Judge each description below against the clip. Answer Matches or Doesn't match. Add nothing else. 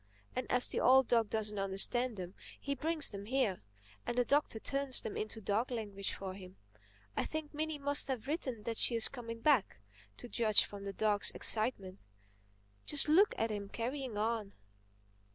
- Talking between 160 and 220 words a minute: Matches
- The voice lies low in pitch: Doesn't match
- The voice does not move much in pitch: Doesn't match